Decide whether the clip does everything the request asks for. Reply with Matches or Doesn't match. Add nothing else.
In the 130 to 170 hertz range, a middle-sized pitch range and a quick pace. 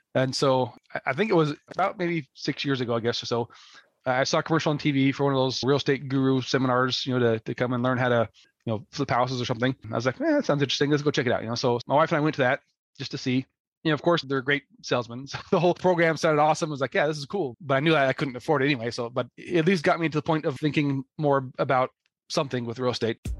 Matches